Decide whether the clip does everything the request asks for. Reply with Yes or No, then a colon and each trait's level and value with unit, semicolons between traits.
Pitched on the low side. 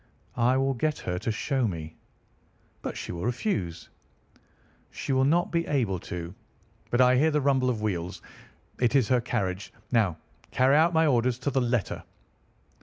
Yes: low, 125 Hz